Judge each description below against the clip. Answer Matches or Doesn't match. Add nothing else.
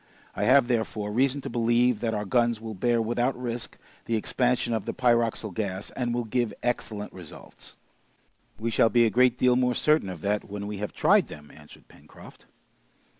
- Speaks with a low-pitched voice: Matches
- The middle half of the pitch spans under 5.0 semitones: Matches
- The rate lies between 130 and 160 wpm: Doesn't match